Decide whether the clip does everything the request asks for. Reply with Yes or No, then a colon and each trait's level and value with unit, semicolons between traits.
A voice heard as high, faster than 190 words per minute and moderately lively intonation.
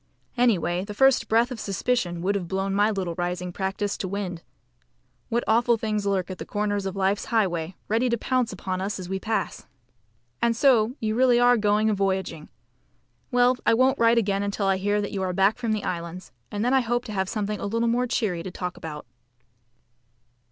Yes: high, 205 Hz; fast, 205 wpm; average, 3.5 semitones